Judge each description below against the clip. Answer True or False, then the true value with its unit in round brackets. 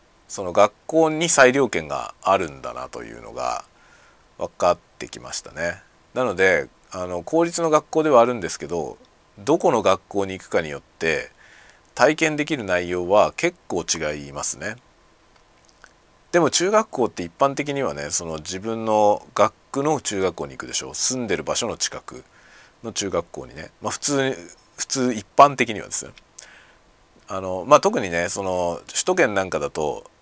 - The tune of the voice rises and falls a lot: True (8.8 semitones)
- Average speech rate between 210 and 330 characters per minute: True (305 characters per minute)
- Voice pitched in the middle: False (115 Hz)